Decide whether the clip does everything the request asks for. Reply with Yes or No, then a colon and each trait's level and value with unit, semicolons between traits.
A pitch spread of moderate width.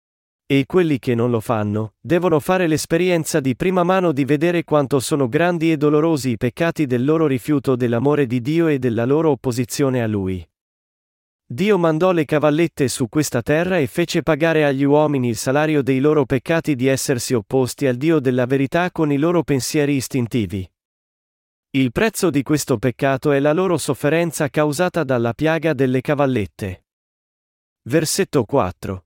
Yes: average, 4.1 semitones